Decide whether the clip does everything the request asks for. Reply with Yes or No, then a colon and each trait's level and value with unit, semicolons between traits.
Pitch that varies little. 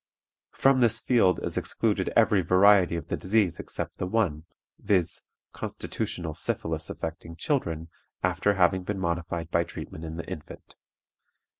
No: average, 3.6 semitones